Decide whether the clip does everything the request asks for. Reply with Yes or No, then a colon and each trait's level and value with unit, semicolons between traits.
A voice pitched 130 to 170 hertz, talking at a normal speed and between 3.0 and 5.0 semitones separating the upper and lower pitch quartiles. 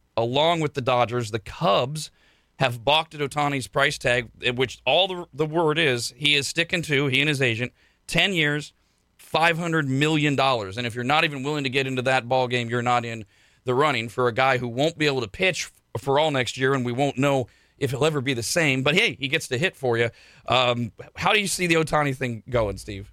No: low, 135 Hz; fast, 230 wpm; average, 3.7 semitones